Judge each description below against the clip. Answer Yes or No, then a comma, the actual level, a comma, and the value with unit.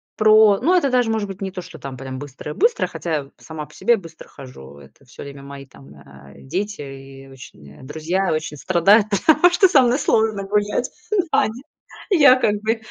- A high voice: No, medium, 175 Hz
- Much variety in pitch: Yes, wide, 8.3 semitones